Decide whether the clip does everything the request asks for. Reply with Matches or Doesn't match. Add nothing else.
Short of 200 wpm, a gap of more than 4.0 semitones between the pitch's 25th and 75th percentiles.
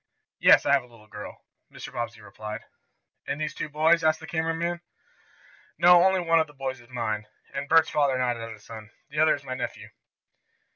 Doesn't match